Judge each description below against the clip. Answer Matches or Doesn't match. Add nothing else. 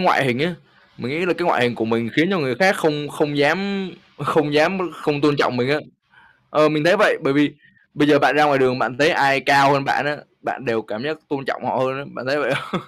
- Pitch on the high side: Doesn't match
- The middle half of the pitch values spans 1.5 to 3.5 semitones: Matches